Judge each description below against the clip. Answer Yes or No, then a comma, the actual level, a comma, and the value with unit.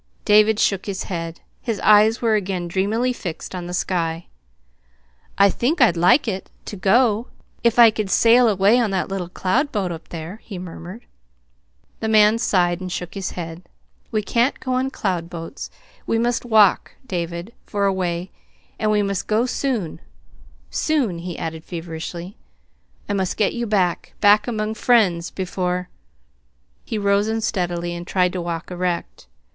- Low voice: No, high, 195 Hz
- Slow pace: No, average, 165 wpm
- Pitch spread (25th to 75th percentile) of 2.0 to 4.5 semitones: Yes, average, 4.0 semitones